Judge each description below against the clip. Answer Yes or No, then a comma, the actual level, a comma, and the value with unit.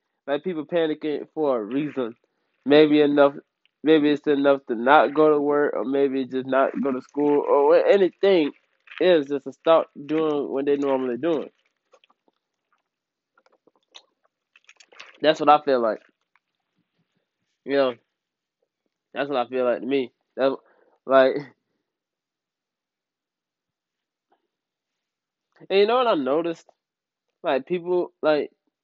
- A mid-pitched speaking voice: Yes, medium, 145 Hz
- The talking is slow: Yes, slow, 125 wpm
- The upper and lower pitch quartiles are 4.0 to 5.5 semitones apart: No, average, 2.8 semitones